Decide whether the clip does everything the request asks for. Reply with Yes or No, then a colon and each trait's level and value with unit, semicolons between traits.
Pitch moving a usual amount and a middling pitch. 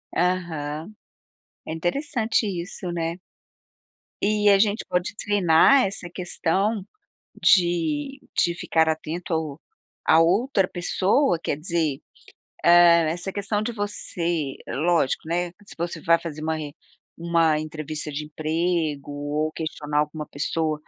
Yes: average, 3.3 semitones; medium, 170 Hz